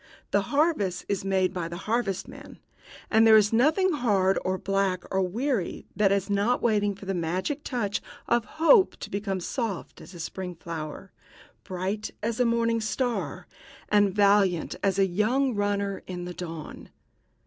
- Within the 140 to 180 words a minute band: Yes, average, 160 wpm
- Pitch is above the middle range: Yes, high, 200 Hz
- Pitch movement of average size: Yes, average, 3.7 semitones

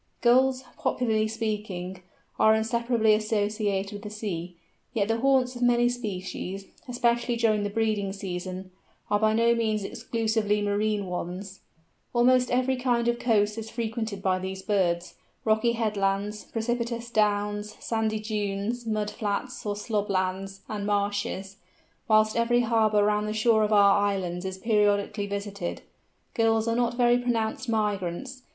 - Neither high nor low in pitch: No, high, 215 Hz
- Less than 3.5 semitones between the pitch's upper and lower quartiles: Yes, narrow, 2.5 semitones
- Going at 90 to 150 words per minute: Yes, average, 140 wpm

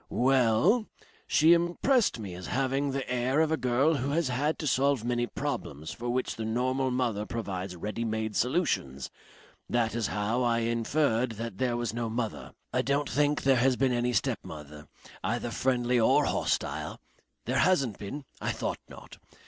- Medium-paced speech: Yes, average, 170 wpm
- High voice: No, low, 120 Hz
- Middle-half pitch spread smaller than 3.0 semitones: No, average, 3.5 semitones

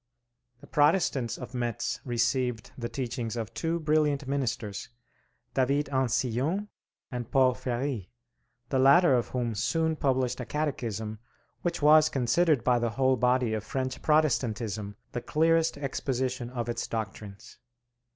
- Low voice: Yes, low, 130 Hz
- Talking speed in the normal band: No, slow, 130 wpm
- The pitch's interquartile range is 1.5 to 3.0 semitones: No, average, 3.6 semitones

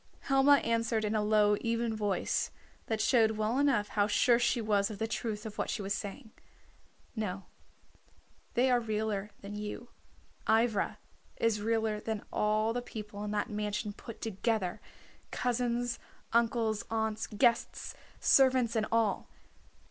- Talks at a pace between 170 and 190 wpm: No, average, 145 wpm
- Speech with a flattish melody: Yes, narrow, 2.0 semitones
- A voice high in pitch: Yes, high, 220 Hz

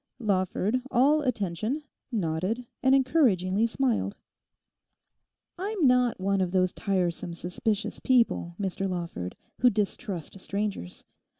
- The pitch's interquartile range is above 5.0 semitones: Yes, wide, 5.4 semitones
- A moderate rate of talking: No, slow, 105 wpm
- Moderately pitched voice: No, high, 205 Hz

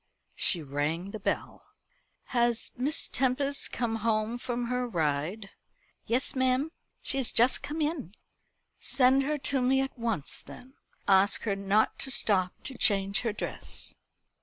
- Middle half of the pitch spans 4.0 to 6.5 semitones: Yes, average, 4.9 semitones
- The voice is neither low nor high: No, high, 235 Hz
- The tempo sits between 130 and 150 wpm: Yes, average, 145 wpm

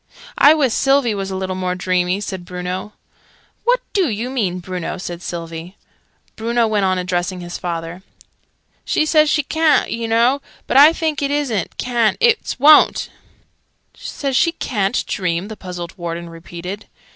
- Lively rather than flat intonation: Yes, wide, 7.1 semitones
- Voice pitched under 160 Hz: No, high, 200 Hz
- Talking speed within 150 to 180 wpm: Yes, average, 155 wpm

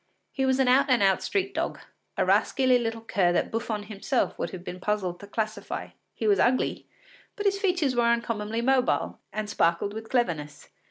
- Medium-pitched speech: No, high, 230 Hz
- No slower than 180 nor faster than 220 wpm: Yes, average, 185 wpm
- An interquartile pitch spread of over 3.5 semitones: Yes, average, 4.2 semitones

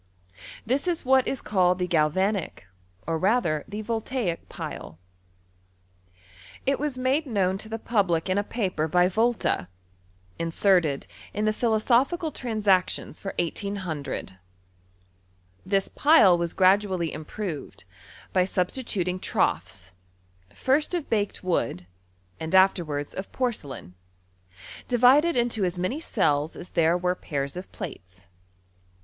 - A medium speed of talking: No, slow, 120 wpm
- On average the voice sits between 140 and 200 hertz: Yes, high, 190 Hz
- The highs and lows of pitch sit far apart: Yes, wide, 5.8 semitones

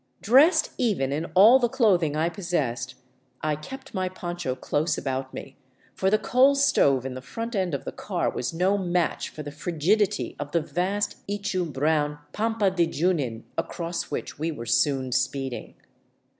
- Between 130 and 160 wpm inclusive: No, average, 170 wpm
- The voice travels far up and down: Yes, wide, 6.1 semitones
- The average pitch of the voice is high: No, medium, 170 Hz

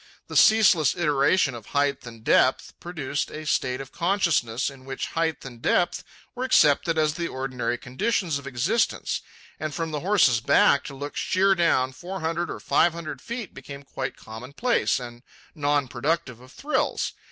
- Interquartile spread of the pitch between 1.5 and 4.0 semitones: No, average, 4.7 semitones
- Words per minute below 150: No, average, 165 wpm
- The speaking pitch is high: No, medium, 145 Hz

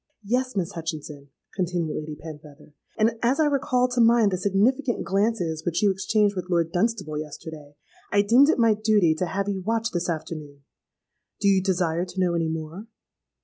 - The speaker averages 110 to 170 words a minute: No, average, 180 wpm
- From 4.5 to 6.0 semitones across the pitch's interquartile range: Yes, wide, 5.4 semitones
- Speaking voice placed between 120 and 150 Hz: No, high, 190 Hz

